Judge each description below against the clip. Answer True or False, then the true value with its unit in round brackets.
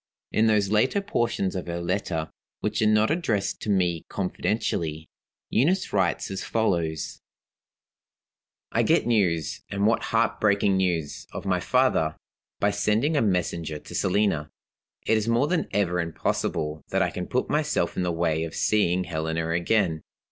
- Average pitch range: True (4.5 semitones)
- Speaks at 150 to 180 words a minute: True (155 wpm)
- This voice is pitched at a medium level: False (95 Hz)